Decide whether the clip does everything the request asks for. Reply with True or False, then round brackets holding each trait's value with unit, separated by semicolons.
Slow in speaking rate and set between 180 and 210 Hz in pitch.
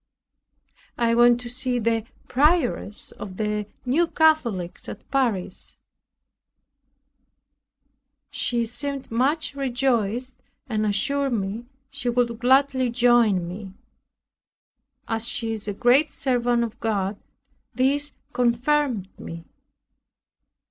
False (100 wpm; 240 Hz)